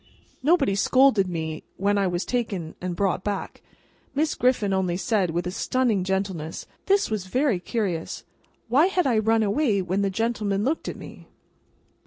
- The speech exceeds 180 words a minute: No, average, 165 wpm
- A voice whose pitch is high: Yes, high, 200 Hz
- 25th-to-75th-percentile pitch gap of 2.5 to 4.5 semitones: No, average, 5.0 semitones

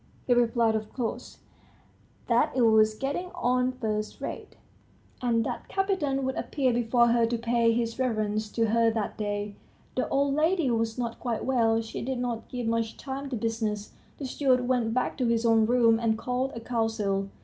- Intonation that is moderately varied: No, narrow, 2.2 semitones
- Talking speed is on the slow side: No, average, 180 wpm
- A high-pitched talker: Yes, high, 235 Hz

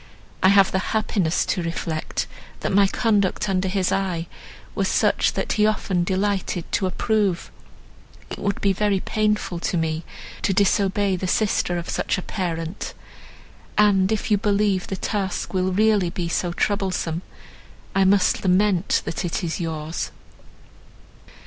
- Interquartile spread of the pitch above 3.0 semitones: No, narrow, 2.5 semitones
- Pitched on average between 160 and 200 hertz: Yes, high, 190 Hz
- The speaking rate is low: No, average, 150 wpm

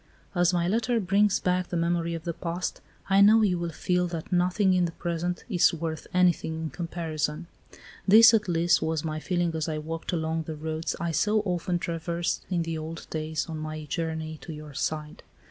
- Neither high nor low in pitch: Yes, medium, 170 Hz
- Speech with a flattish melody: Yes, narrow, 2.1 semitones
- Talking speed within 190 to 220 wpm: Yes, average, 195 wpm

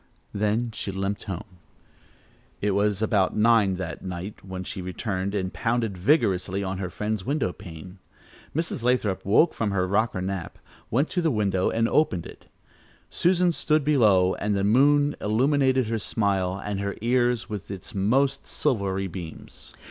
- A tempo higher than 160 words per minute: No, average, 155 wpm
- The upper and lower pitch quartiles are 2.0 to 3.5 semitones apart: No, average, 4.2 semitones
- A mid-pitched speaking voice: No, low, 105 Hz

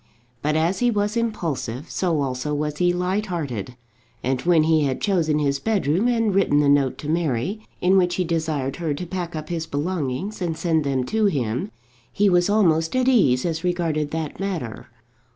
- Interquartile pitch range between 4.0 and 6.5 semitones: Yes, average, 4.5 semitones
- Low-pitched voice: No, medium, 165 Hz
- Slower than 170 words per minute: No, average, 190 wpm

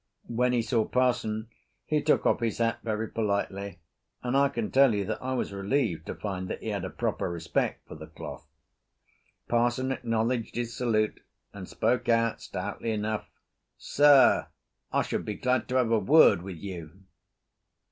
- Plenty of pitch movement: No, average, 3.7 semitones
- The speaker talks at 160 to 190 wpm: Yes, average, 170 wpm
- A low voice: Yes, low, 115 Hz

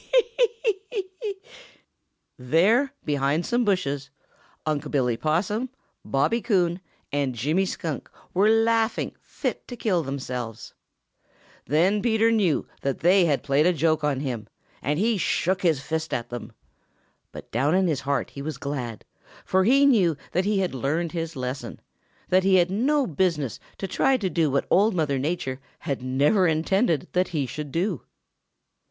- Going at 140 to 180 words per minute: Yes, average, 165 wpm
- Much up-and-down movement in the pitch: Yes, wide, 6.2 semitones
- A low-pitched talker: No, medium, 165 Hz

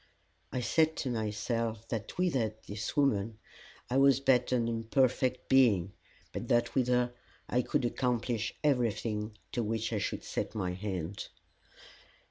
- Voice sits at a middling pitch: No, low, 115 Hz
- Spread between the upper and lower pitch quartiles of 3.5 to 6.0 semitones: No, average, 3.0 semitones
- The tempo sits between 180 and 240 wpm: No, average, 140 wpm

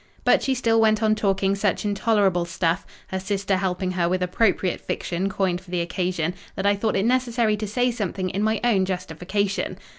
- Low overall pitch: No, high, 195 Hz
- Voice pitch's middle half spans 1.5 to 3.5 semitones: Yes, average, 2.8 semitones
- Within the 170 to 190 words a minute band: Yes, average, 180 wpm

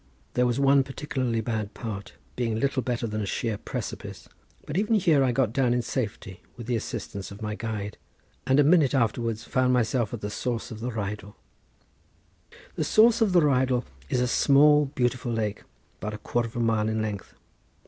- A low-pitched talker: Yes, low, 120 Hz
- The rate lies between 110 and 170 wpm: No, average, 190 wpm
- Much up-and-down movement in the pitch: No, average, 3.6 semitones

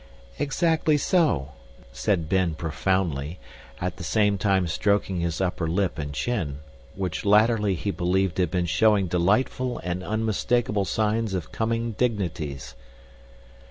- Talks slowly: Yes, slow, 125 wpm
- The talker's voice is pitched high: No, very low, 95 Hz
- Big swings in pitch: No, average, 4.3 semitones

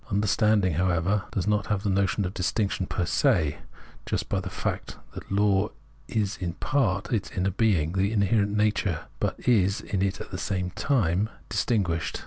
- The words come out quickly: No, average, 175 wpm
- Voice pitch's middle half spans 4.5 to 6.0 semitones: No, narrow, 2.5 semitones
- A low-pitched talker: Yes, low, 100 Hz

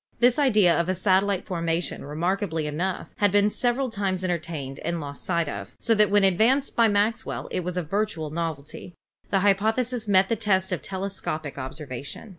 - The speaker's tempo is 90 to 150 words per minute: No, average, 180 wpm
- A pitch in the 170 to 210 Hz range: Yes, high, 190 Hz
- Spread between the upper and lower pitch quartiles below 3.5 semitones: No, average, 4.1 semitones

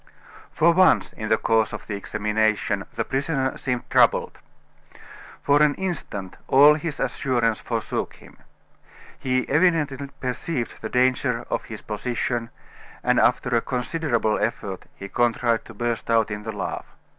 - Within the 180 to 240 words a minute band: No, average, 145 wpm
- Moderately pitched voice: No, low, 120 Hz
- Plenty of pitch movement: No, average, 4.0 semitones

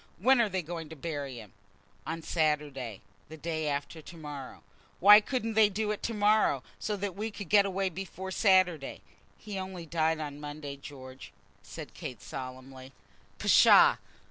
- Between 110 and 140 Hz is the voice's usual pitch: No, medium, 165 Hz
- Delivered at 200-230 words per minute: No, average, 165 wpm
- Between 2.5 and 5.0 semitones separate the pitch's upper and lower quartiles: No, wide, 5.6 semitones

